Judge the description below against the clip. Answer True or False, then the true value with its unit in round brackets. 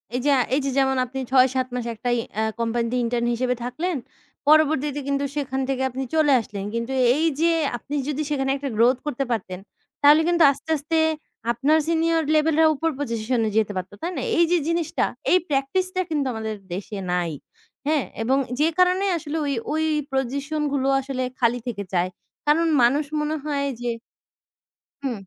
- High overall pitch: True (275 Hz)